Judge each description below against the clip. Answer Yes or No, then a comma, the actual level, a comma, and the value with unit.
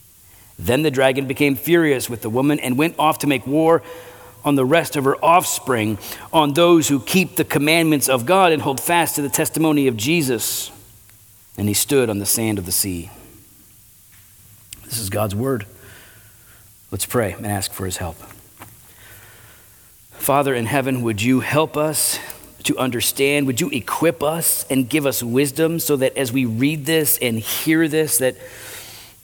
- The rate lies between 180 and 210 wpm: No, average, 170 wpm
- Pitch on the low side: Yes, low, 130 Hz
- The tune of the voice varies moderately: No, wide, 5.7 semitones